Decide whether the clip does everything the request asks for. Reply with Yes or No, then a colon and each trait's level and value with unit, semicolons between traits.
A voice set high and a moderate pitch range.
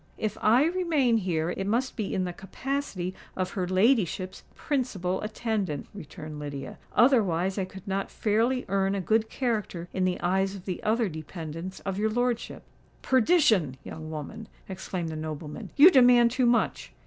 Yes: high, 195 Hz; average, 5.0 semitones